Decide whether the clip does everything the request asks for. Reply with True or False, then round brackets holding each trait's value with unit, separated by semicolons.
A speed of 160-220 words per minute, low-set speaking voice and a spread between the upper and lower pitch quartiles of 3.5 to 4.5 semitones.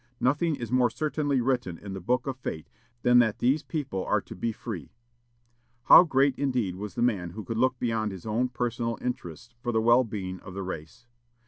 True (205 wpm; 120 Hz; 4.1 semitones)